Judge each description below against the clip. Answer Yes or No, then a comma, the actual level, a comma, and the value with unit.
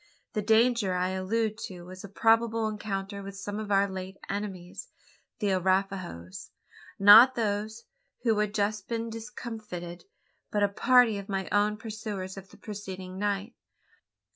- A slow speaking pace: No, average, 145 wpm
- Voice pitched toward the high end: Yes, high, 205 Hz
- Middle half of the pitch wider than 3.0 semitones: No, narrow, 2.4 semitones